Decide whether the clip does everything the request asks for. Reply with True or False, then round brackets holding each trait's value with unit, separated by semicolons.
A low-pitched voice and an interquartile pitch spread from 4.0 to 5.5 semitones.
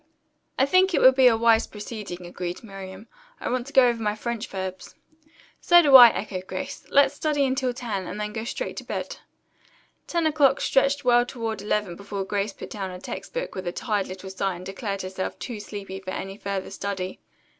False (210 Hz; 4.9 semitones)